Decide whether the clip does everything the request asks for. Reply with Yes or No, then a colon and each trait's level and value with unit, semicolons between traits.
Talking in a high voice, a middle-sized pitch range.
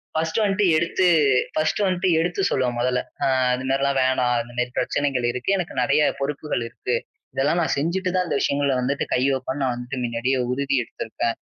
No: medium, 140 Hz; average, 4.6 semitones